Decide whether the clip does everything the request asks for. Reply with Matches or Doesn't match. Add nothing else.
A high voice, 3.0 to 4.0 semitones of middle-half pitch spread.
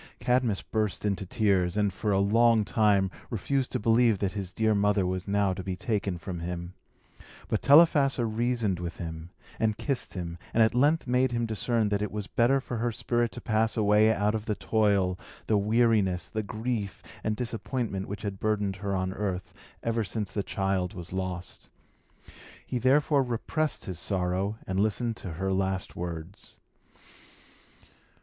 Doesn't match